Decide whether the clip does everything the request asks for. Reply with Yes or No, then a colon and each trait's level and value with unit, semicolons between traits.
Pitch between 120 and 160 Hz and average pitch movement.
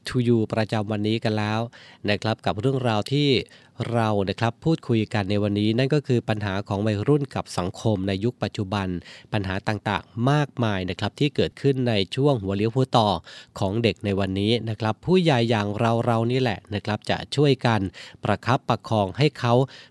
No: low, 110 Hz; average, 3.4 semitones